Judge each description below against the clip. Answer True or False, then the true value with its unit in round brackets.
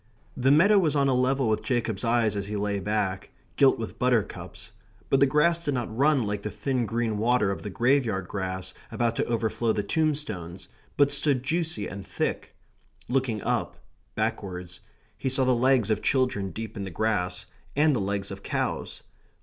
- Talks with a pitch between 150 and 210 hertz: False (115 Hz)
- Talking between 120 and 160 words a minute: False (180 wpm)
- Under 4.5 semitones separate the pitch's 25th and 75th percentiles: False (4.8 semitones)